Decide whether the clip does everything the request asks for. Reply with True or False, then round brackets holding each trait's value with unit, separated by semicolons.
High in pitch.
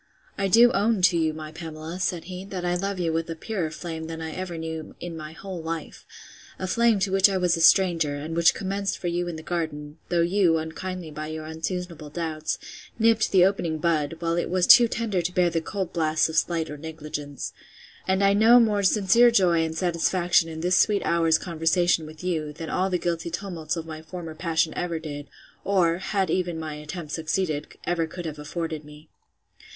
False (170 Hz)